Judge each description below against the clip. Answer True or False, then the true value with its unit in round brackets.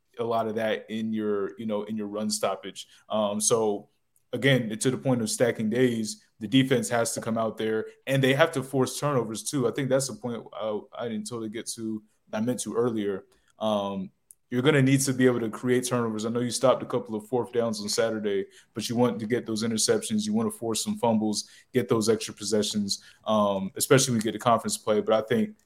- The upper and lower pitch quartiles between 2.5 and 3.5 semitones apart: True (2.8 semitones)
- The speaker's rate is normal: False (235 wpm)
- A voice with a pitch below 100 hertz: False (115 Hz)